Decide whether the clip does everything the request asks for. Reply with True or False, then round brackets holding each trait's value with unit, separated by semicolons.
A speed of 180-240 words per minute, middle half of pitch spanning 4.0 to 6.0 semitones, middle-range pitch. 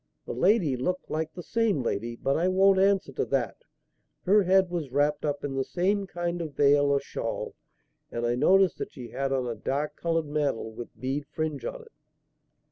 True (200 wpm; 5.4 semitones; 150 Hz)